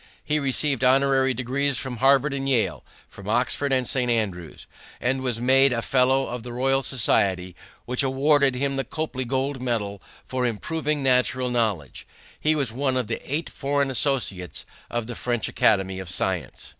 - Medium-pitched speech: No, low, 130 Hz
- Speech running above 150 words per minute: Yes, average, 170 wpm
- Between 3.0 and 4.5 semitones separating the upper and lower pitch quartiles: No, narrow, 2.5 semitones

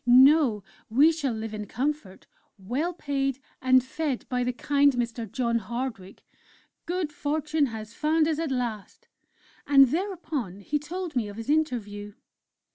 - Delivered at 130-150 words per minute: Yes, average, 145 wpm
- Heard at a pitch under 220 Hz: No, very high, 265 Hz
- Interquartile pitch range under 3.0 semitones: No, average, 5.2 semitones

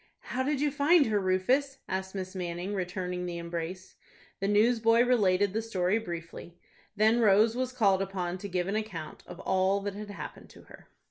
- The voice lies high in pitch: Yes, high, 195 Hz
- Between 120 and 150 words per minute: No, average, 185 wpm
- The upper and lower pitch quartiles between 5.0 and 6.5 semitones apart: No, average, 3.7 semitones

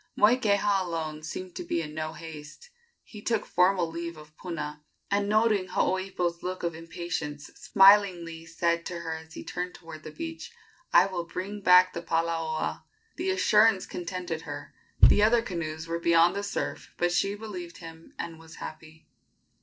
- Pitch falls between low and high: Yes, medium, 170 Hz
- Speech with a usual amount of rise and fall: Yes, average, 3.3 semitones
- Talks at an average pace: Yes, average, 165 wpm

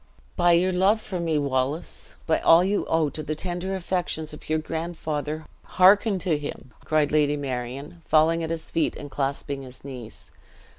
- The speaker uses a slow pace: No, average, 170 wpm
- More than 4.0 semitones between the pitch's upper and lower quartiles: No, average, 3.3 semitones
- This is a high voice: No, medium, 155 Hz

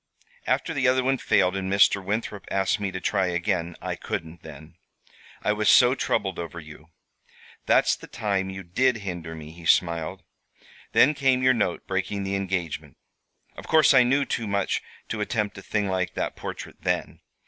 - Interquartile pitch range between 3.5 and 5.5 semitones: Yes, average, 4.1 semitones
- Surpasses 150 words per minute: Yes, average, 180 wpm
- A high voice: No, very low, 95 Hz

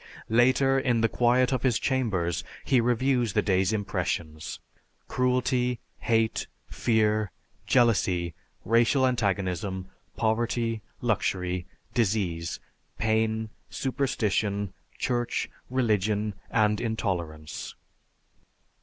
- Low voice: Yes, low, 110 Hz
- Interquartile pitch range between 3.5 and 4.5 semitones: Yes, average, 4.0 semitones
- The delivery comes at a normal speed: No, slow, 85 wpm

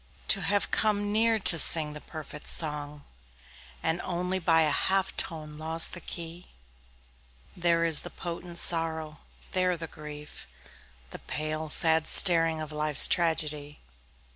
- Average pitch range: No, narrow, 2.3 semitones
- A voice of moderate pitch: Yes, medium, 165 Hz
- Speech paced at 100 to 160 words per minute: Yes, average, 140 wpm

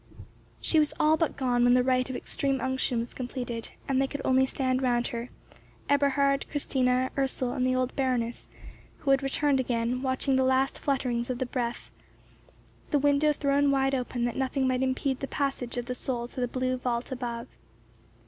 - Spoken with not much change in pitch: Yes, narrow, 1.7 semitones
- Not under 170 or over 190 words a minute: Yes, average, 185 wpm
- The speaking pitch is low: No, very high, 260 Hz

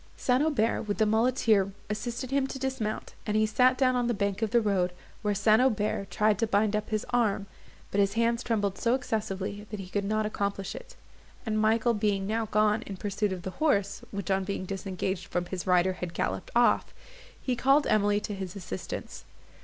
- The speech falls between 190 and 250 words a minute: Yes, average, 200 wpm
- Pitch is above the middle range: Yes, high, 210 Hz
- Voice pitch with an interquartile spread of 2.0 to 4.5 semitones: Yes, average, 2.8 semitones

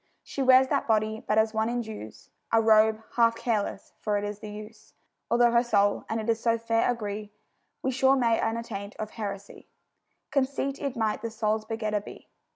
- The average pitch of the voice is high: Yes, high, 220 Hz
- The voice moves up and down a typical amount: No, narrow, 1.9 semitones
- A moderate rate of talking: Yes, average, 180 wpm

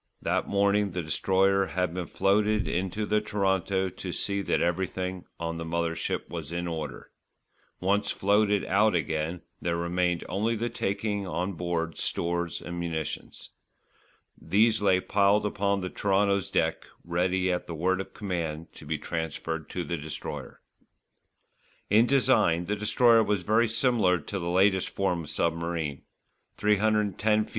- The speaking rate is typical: Yes, average, 150 wpm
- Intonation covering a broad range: No, average, 3.2 semitones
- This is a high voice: No, very low, 95 Hz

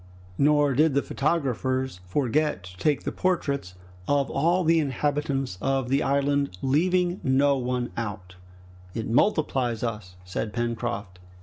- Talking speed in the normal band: No, slow, 130 wpm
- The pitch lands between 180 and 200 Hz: No, low, 135 Hz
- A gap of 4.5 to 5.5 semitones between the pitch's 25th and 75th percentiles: No, average, 3.7 semitones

